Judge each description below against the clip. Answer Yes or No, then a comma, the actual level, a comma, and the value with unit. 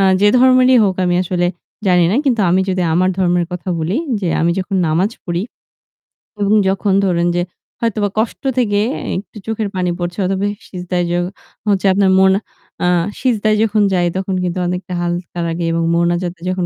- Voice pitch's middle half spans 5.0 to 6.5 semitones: No, narrow, 2.6 semitones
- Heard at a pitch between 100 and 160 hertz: No, medium, 185 Hz